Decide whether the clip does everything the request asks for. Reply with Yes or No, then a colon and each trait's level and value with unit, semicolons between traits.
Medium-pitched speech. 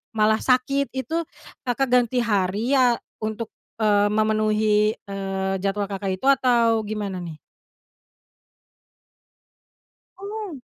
No: high, 215 Hz